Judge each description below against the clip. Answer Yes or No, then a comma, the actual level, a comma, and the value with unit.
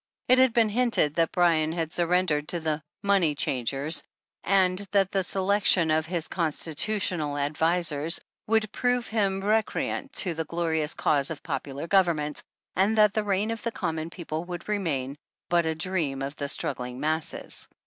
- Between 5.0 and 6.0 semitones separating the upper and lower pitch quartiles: No, average, 4.3 semitones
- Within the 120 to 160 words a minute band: No, average, 170 wpm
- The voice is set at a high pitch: No, medium, 170 Hz